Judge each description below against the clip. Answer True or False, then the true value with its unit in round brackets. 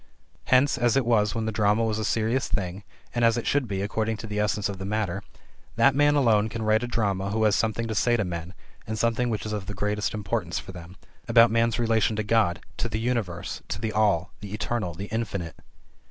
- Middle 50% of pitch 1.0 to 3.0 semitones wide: True (2.4 semitones)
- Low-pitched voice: True (110 Hz)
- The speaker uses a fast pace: True (230 wpm)